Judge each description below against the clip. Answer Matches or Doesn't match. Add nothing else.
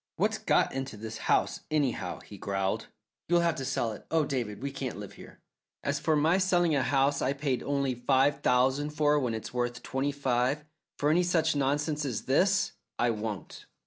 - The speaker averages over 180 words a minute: Matches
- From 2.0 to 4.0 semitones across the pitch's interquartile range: Matches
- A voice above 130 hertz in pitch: Matches